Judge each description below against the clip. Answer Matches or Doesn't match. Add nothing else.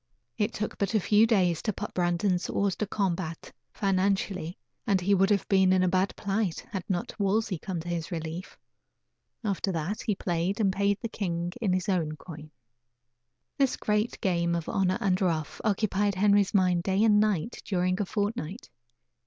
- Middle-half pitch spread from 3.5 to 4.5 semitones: Doesn't match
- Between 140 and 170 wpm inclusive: Doesn't match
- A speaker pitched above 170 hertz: Matches